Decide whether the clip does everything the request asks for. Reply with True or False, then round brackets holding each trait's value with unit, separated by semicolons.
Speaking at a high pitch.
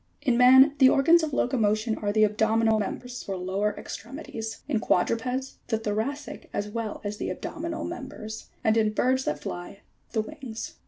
True (225 Hz)